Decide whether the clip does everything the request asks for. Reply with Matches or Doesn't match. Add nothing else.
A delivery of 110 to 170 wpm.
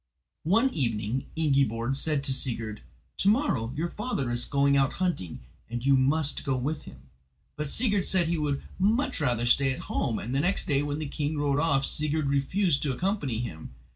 Doesn't match